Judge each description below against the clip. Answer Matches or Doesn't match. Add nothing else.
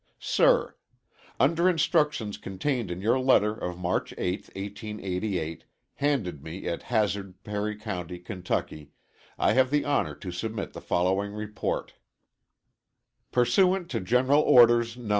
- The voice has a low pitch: Matches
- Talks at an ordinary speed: Doesn't match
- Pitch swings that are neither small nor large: Doesn't match